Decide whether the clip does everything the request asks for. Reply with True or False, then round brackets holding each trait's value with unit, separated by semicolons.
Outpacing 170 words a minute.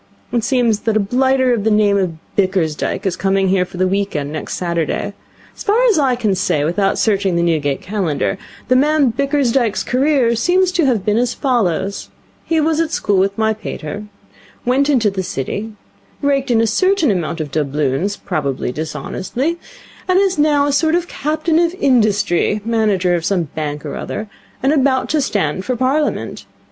True (180 wpm)